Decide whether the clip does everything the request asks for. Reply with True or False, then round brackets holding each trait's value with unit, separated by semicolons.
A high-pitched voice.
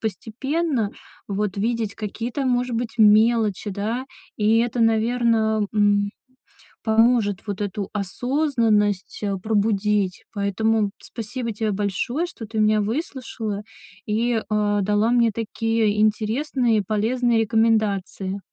True (220 Hz)